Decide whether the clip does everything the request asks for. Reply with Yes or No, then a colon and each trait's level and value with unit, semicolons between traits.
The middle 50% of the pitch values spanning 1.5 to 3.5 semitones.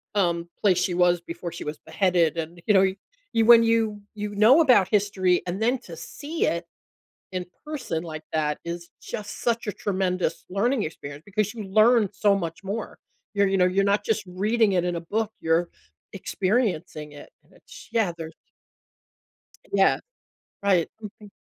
No: average, 3.9 semitones